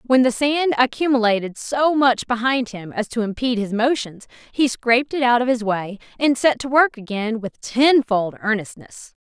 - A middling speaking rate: Yes, average, 180 wpm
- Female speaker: Yes, female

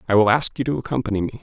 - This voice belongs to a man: Yes, male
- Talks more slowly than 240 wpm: No, fast, 295 wpm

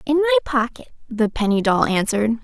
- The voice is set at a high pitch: Yes, high, 230 Hz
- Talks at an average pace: Yes, average, 170 wpm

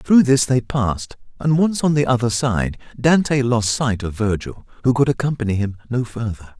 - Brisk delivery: No, average, 190 wpm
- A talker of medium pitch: No, low, 120 Hz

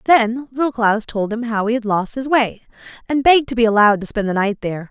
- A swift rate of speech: Yes, fast, 255 wpm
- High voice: Yes, high, 230 Hz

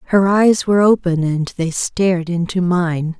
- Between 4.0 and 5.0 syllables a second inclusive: Yes, 4.5 syllables/s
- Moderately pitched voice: Yes, medium, 175 Hz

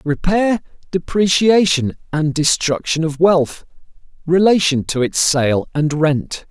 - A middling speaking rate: No, slow, 110 wpm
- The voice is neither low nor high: Yes, medium, 160 Hz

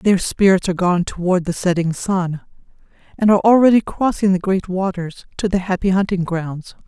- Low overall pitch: No, medium, 185 Hz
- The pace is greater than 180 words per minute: No, average, 175 wpm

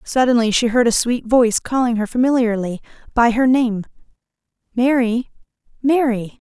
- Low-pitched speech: No, high, 240 Hz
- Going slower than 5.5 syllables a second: Yes, 5.1 syllables/s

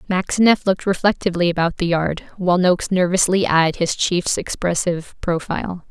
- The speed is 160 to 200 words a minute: No, average, 140 wpm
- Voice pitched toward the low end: No, medium, 180 Hz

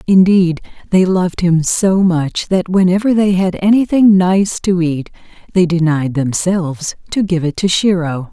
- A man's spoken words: No, female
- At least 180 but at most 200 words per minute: No, average, 160 wpm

